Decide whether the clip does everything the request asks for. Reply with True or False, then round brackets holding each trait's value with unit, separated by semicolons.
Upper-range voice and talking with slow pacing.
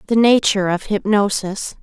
True (205 Hz; 130 wpm)